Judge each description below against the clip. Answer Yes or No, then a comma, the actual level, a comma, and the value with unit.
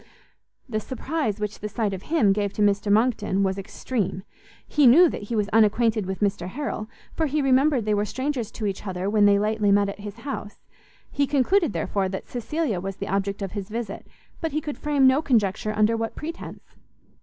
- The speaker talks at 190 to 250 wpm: Yes, average, 200 wpm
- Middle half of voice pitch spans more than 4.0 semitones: Yes, average, 4.6 semitones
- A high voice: Yes, high, 215 Hz